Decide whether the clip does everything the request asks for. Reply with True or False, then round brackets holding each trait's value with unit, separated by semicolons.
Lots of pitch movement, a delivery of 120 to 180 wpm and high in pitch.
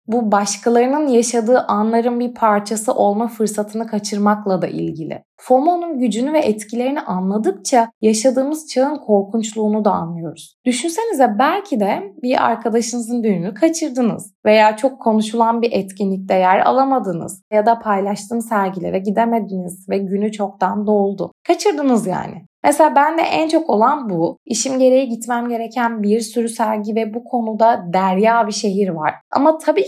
False (3.8 semitones; 135 wpm; 230 Hz)